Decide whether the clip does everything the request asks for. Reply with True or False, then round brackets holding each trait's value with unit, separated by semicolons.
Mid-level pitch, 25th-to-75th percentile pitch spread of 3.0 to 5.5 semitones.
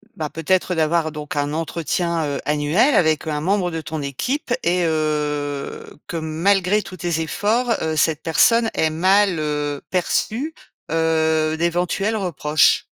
True (160 Hz; 3.3 semitones)